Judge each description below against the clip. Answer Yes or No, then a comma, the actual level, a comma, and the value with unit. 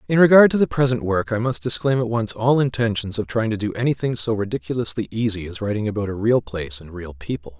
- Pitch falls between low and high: No, low, 110 Hz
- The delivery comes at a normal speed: No, fast, 235 wpm